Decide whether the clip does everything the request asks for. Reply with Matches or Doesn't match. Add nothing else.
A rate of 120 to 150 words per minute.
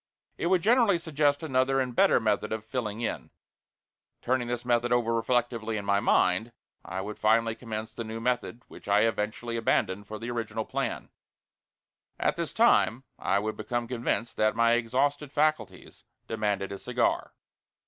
Doesn't match